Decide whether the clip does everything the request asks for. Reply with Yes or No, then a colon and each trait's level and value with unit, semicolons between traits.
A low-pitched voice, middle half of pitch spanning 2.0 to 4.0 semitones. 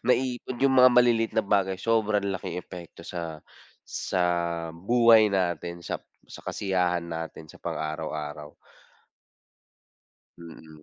No: very low, 90 Hz; wide, 5.7 semitones